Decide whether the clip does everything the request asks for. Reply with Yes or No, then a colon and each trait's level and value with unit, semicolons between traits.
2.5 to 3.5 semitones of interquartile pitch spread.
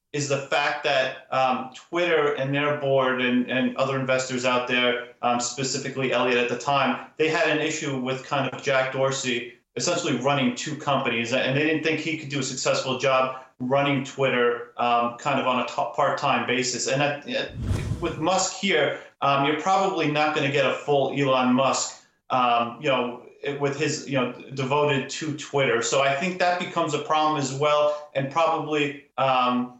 Yes: average, 2.8 semitones